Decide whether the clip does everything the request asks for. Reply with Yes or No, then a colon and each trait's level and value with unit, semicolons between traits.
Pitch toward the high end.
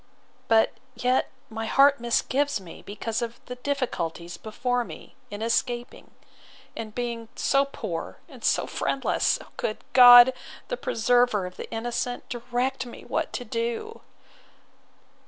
Yes: high, 240 Hz